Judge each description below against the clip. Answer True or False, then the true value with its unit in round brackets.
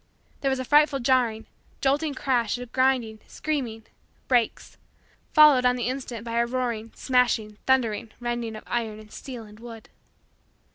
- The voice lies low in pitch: False (245 Hz)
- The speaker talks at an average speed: True (150 wpm)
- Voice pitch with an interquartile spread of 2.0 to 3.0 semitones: True (2.7 semitones)